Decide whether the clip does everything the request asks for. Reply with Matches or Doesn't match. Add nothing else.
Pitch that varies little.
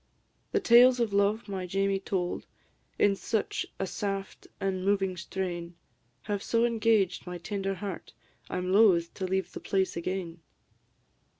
Matches